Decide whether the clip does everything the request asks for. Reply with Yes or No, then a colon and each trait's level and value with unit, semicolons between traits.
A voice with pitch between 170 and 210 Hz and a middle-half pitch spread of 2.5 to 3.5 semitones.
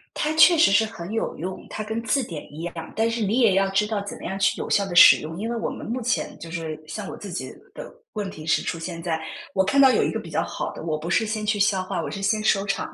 No: high, 200 Hz; average, 4.4 semitones